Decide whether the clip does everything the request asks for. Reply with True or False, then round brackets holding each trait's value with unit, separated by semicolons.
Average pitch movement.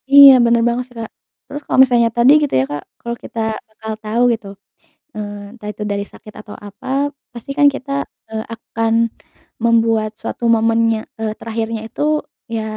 False (1.6 semitones)